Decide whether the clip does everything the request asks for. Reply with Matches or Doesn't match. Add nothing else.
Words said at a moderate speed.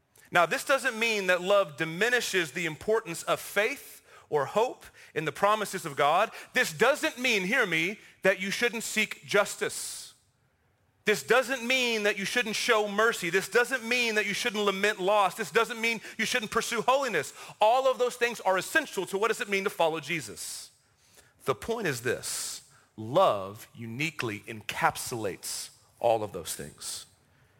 Matches